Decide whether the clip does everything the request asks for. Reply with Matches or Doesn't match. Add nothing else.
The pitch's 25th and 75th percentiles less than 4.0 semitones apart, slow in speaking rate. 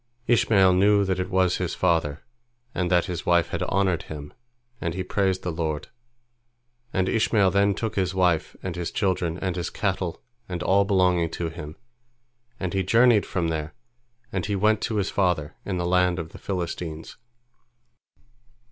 Doesn't match